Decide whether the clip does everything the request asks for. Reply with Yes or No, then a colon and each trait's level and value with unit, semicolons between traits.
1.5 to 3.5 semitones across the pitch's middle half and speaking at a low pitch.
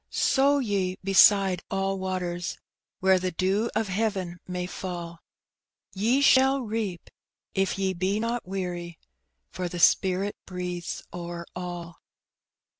No: narrow, 2.4 semitones; medium, 185 Hz